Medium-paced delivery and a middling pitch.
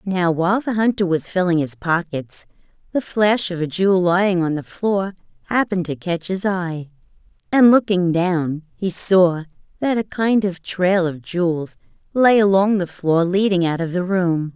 Yes: average, 175 wpm; medium, 180 Hz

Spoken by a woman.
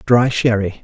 No: male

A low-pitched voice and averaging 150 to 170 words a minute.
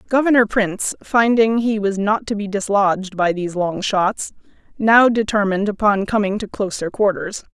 No: high, 205 Hz; average, 160 wpm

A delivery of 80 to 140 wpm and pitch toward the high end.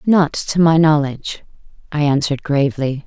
No: slow, 135 wpm; medium, 150 Hz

